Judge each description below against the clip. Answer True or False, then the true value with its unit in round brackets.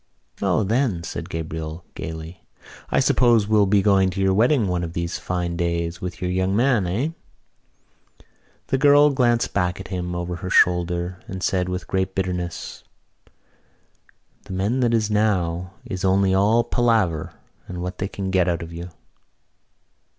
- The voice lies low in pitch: True (95 Hz)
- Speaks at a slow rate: False (160 wpm)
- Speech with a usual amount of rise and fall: True (3.2 semitones)